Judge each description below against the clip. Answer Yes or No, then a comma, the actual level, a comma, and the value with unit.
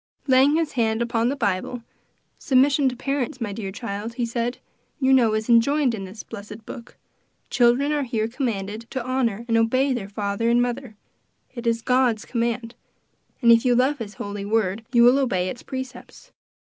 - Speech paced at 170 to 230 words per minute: Yes, average, 180 wpm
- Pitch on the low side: No, high, 235 Hz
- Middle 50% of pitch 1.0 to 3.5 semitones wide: Yes, average, 2.8 semitones